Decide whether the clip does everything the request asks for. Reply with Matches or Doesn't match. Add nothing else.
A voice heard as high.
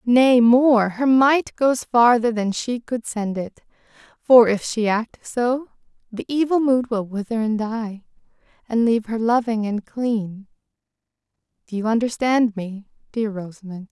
Matches